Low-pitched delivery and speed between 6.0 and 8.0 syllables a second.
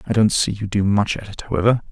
Yes: low, 105 Hz; 6.8 syllables/s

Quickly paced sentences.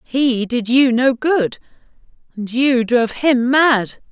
No: average, 145 wpm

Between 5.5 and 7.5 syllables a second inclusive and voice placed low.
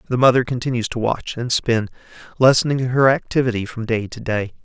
Yes: 5.8 syllables/s; low, 120 Hz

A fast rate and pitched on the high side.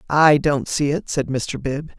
No: fast, 210 wpm; medium, 145 Hz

